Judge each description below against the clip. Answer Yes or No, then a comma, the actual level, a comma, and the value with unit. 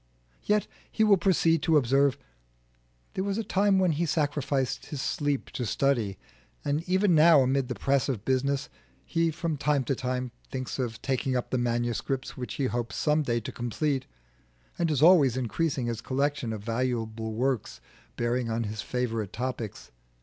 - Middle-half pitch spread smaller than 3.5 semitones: No, average, 4.1 semitones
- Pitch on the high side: No, low, 135 Hz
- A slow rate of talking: No, average, 170 wpm